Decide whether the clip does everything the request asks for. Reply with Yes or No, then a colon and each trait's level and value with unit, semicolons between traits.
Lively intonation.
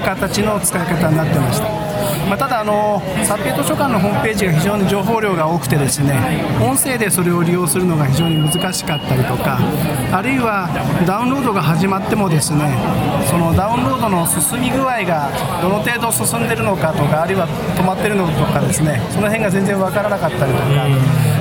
No: average, 4.7 semitones